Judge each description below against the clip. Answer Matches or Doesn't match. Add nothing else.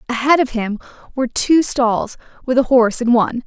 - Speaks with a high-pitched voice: Matches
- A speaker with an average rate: Matches